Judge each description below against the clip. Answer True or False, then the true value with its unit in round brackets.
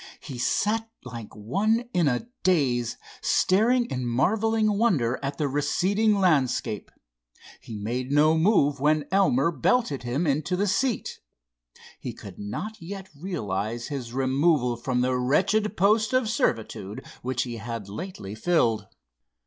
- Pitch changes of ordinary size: False (8.5 semitones)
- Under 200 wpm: True (135 wpm)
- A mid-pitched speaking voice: True (145 Hz)